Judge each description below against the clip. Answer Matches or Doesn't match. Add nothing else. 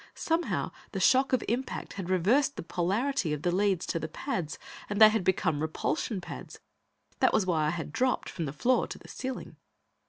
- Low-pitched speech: Doesn't match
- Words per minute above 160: Matches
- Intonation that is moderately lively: Doesn't match